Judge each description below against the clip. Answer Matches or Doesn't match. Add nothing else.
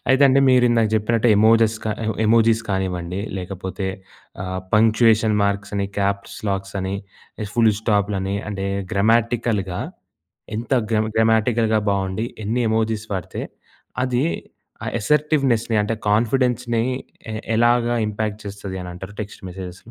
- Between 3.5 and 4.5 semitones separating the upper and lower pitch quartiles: Doesn't match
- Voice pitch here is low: Matches